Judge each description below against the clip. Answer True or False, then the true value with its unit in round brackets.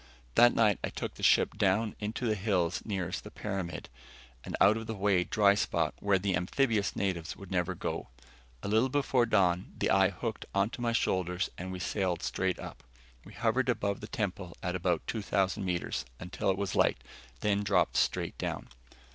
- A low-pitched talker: True (100 Hz)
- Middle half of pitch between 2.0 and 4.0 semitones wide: True (2.9 semitones)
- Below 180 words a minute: False (185 wpm)